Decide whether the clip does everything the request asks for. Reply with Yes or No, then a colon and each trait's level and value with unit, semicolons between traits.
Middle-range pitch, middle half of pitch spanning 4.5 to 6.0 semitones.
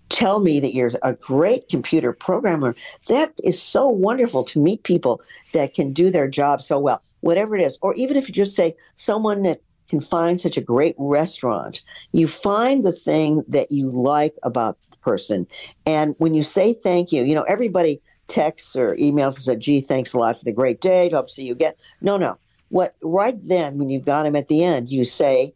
Yes: medium, 160 Hz; average, 4.8 semitones